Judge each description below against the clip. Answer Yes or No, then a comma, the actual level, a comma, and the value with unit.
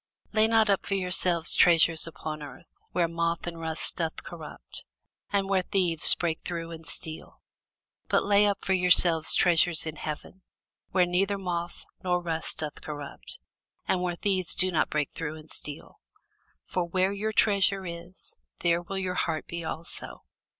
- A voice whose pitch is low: No, medium, 175 Hz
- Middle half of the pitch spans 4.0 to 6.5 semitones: No, narrow, 2.5 semitones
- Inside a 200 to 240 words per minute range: No, average, 165 wpm